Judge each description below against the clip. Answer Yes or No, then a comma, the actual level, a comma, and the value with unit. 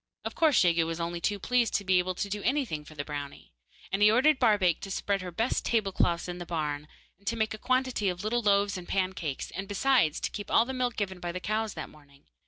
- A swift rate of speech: Yes, fast, 250 wpm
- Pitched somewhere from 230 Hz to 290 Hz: No, high, 195 Hz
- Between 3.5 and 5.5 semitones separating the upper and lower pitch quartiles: Yes, average, 4.4 semitones